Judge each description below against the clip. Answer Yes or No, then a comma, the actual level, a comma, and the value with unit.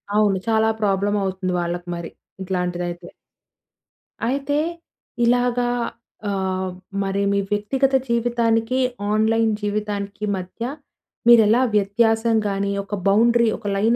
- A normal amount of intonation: Yes, average, 3.2 semitones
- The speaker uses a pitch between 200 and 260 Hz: Yes, high, 210 Hz